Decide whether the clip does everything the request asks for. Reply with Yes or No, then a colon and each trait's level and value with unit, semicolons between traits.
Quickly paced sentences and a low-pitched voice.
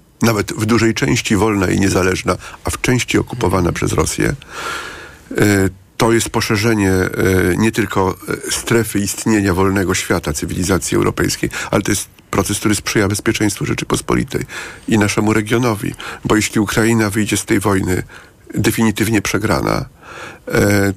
No: average, 130 wpm; low, 105 Hz